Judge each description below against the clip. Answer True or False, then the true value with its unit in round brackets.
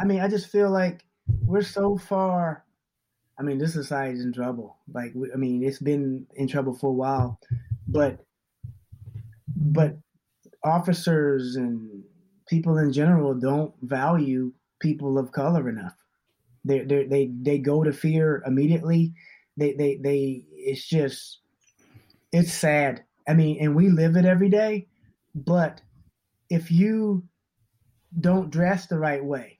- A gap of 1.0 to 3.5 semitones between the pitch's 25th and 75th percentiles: False (4.5 semitones)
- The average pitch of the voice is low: False (145 Hz)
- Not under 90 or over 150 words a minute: True (145 wpm)